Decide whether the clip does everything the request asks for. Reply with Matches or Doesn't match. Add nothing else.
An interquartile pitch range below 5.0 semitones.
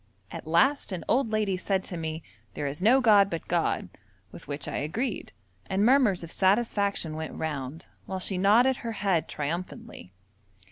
Doesn't match